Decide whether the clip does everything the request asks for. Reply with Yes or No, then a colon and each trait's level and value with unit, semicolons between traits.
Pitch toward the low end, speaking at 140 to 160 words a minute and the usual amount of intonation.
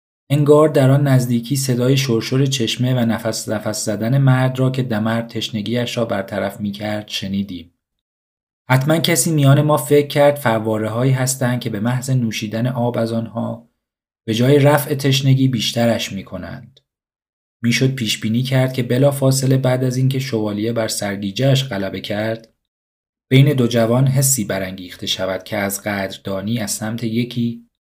Yes: low, 115 Hz; average, 150 wpm; average, 3.5 semitones